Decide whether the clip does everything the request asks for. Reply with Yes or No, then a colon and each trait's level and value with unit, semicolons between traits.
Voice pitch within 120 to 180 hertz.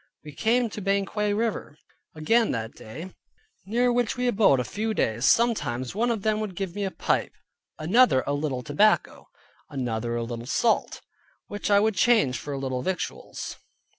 No: high, 195 Hz